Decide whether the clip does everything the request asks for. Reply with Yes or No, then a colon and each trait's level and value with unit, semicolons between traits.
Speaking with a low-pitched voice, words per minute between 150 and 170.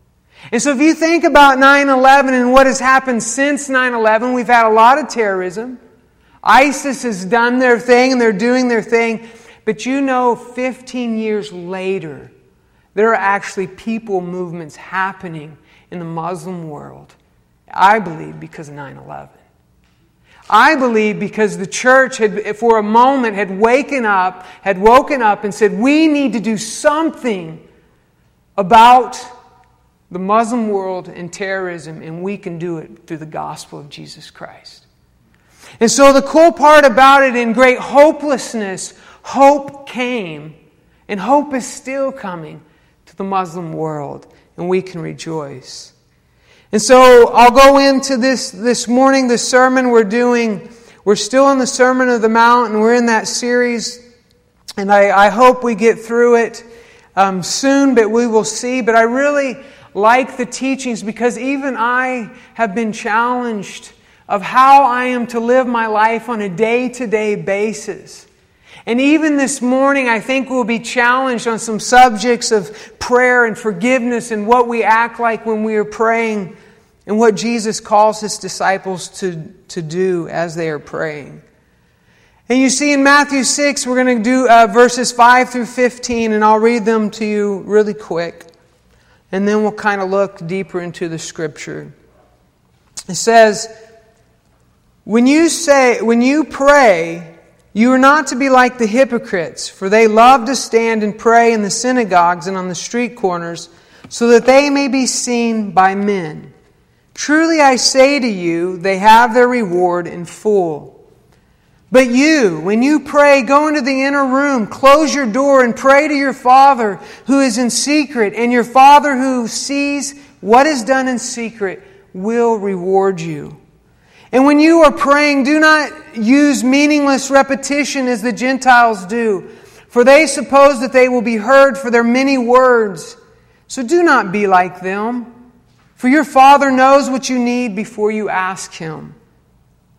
No: high, 235 Hz; average, 160 wpm